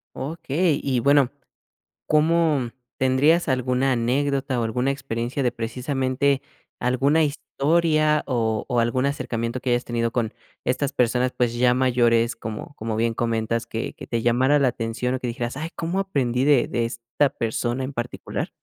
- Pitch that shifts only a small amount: No, average, 3.1 semitones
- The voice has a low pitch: Yes, low, 125 Hz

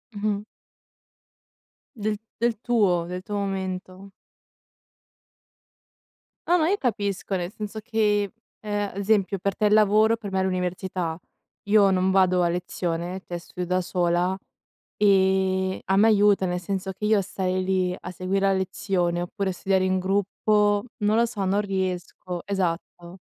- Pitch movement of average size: No, narrow, 2.1 semitones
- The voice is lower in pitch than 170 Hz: No, high, 190 Hz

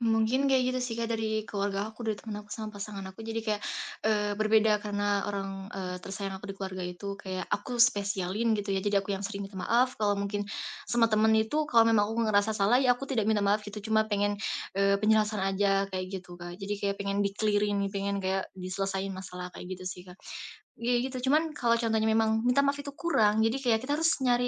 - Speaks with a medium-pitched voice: No, high, 210 Hz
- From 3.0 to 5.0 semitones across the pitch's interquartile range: No, narrow, 2.4 semitones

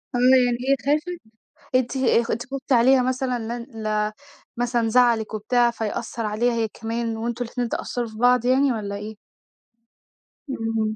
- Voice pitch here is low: No, high, 235 Hz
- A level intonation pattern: Yes, narrow, 2.0 semitones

